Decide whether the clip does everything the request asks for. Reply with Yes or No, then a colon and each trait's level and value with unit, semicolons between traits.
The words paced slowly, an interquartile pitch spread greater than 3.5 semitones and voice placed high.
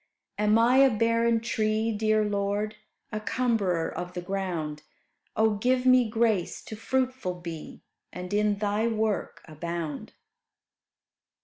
Yes: slow, 125 wpm; average, 4.0 semitones; high, 215 Hz